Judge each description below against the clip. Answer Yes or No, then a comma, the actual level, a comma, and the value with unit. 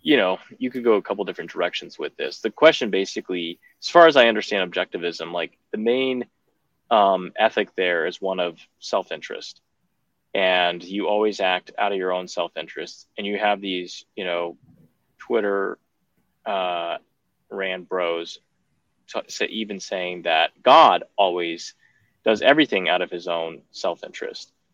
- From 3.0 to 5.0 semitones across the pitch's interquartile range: No, narrow, 2.6 semitones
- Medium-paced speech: Yes, average, 160 wpm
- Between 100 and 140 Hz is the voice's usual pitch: No, very low, 90 Hz